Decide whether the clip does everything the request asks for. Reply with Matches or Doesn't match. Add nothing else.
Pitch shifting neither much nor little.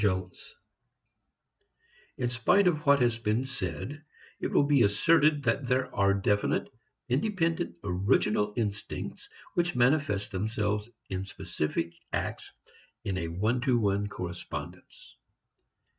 Doesn't match